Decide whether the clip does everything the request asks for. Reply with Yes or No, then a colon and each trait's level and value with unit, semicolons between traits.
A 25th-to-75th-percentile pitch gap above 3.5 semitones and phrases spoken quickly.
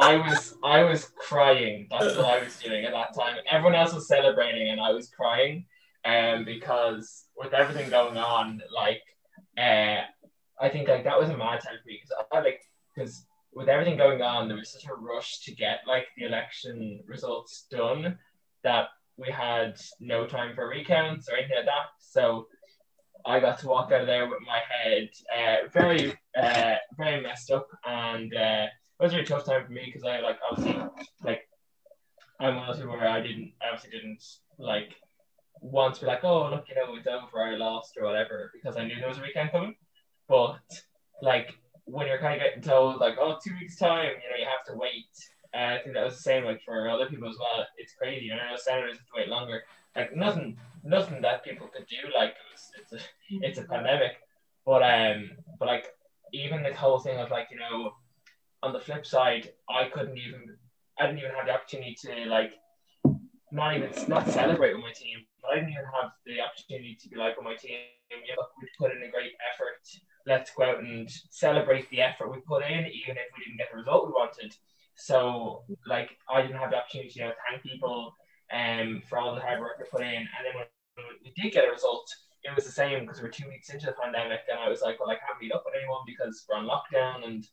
Yes: average, 4.6 semitones; fast, 225 wpm